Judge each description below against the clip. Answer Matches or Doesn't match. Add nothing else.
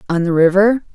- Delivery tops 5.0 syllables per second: Matches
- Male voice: Doesn't match